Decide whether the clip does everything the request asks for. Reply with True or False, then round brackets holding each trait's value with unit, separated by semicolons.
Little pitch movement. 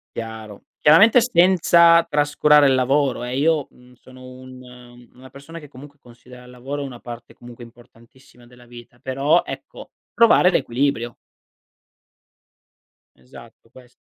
False (3.2 semitones)